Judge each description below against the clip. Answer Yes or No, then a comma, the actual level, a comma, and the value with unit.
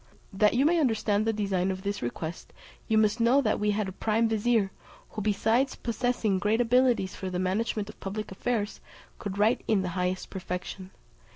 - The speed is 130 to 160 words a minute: No, average, 185 wpm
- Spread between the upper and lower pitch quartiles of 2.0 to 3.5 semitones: Yes, average, 3.0 semitones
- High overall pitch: Yes, high, 210 Hz